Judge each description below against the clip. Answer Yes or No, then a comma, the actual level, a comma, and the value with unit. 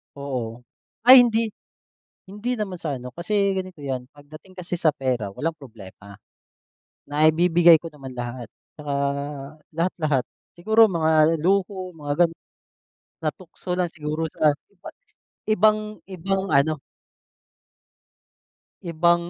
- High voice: No, medium, 165 Hz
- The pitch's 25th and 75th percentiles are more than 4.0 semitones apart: Yes, average, 4.5 semitones